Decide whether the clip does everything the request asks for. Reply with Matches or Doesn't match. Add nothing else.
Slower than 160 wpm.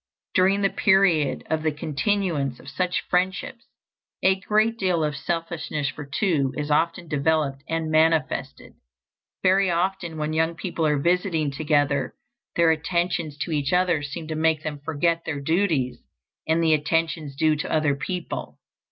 Matches